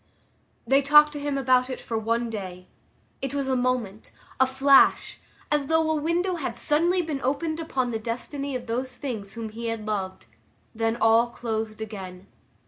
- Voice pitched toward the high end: Yes, very high, 255 Hz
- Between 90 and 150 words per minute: No, average, 175 wpm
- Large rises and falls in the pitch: No, average, 4.2 semitones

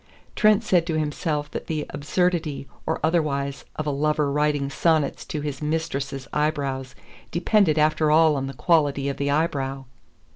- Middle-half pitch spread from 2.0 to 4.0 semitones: Yes, narrow, 2.4 semitones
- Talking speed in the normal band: Yes, average, 155 wpm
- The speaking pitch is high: No, medium, 150 Hz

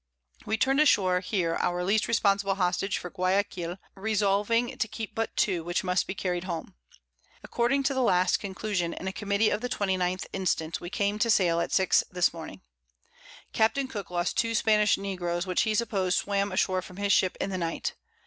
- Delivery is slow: No, average, 185 wpm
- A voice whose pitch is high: Yes, high, 195 Hz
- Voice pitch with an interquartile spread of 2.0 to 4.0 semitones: Yes, average, 2.9 semitones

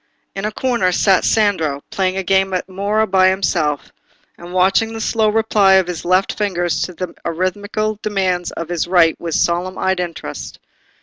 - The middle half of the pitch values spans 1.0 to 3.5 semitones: Yes, narrow, 2.6 semitones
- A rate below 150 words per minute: No, average, 175 wpm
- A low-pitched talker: No, medium, 185 Hz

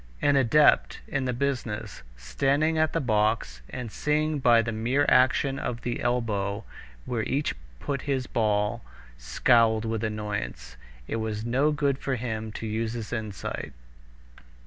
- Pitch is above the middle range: No, low, 115 Hz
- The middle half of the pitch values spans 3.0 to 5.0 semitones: Yes, average, 4.0 semitones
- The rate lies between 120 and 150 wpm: Yes, average, 145 wpm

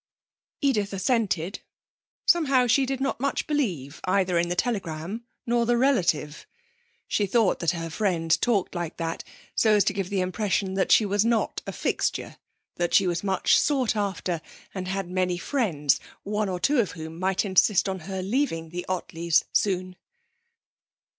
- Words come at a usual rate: Yes, average, 165 wpm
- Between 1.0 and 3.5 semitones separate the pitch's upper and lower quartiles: No, average, 4.5 semitones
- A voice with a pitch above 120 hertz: Yes, high, 190 Hz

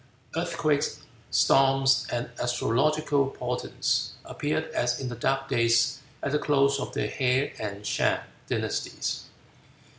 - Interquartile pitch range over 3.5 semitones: No, narrow, 2.4 semitones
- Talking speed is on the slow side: Yes, slow, 120 wpm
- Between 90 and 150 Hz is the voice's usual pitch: Yes, low, 135 Hz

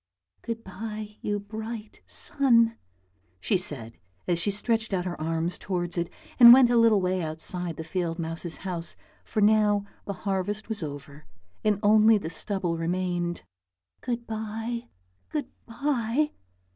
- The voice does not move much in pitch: No, average, 4.4 semitones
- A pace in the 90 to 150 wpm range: Yes, average, 145 wpm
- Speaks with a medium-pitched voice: No, high, 200 Hz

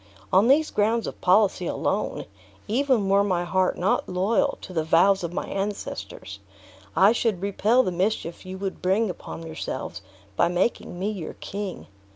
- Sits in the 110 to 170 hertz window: No, high, 190 Hz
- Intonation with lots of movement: No, average, 2.9 semitones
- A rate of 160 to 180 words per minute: Yes, average, 165 wpm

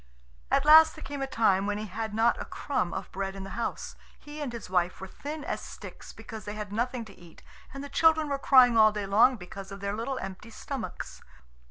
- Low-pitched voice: No, high, 225 Hz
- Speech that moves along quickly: Yes, fast, 230 wpm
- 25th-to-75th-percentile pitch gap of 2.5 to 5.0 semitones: No, wide, 5.6 semitones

